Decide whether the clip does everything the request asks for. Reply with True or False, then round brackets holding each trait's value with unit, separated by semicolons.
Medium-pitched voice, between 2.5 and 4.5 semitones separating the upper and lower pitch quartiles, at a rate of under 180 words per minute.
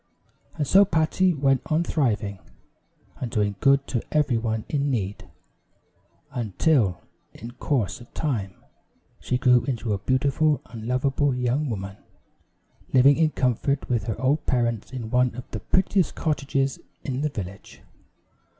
False (125 Hz; 4.2 semitones; 140 wpm)